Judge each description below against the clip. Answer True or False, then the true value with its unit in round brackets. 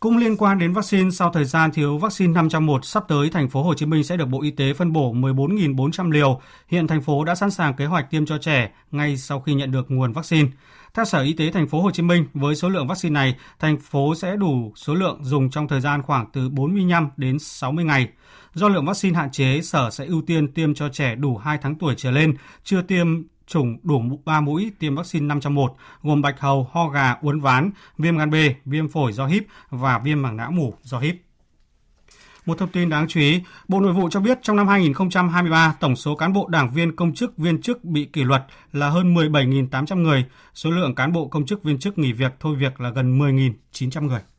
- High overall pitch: False (150 Hz)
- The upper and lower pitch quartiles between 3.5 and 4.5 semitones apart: True (3.8 semitones)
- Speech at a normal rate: True (230 wpm)